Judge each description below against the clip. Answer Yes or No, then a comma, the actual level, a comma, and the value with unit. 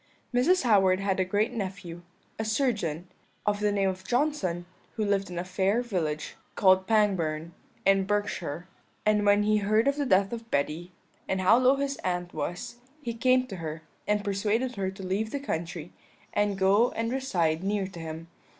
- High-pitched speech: Yes, high, 200 Hz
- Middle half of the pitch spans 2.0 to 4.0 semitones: Yes, average, 3.7 semitones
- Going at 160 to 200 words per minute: Yes, average, 180 wpm